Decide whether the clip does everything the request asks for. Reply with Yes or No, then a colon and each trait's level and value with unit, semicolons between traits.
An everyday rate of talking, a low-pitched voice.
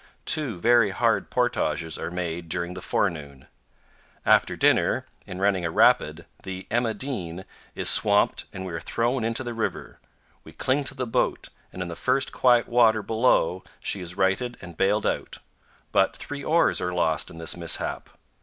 Yes: average, 175 wpm; very low, 95 Hz